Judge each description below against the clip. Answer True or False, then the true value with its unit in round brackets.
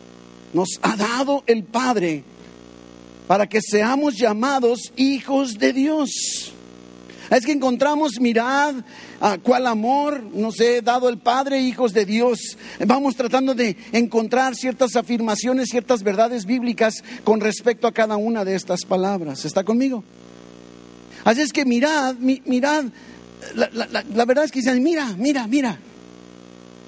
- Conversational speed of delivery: True (135 wpm)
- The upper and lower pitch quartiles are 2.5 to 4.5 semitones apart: False (5.3 semitones)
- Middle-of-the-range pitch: False (235 Hz)